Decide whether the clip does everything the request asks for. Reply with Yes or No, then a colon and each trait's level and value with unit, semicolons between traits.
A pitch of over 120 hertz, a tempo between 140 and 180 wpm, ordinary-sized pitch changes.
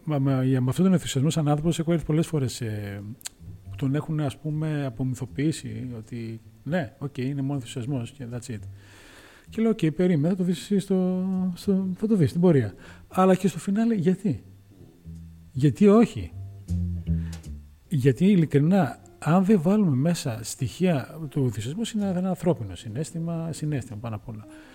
No: medium, 140 Hz; average, 155 wpm; wide, 8.0 semitones